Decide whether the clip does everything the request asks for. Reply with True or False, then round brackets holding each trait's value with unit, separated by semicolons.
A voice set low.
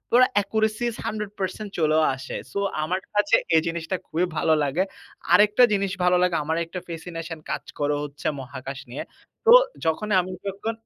False (180 Hz)